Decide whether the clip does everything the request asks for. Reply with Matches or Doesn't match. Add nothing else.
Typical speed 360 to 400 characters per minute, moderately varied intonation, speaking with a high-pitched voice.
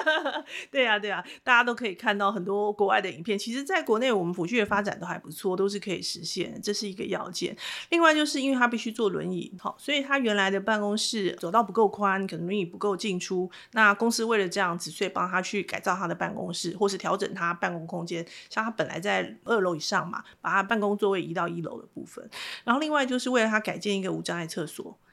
Matches